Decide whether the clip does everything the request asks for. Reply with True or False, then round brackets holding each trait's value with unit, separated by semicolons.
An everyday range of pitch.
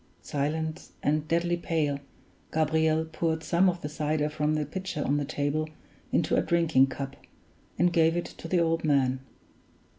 False (2.1 semitones)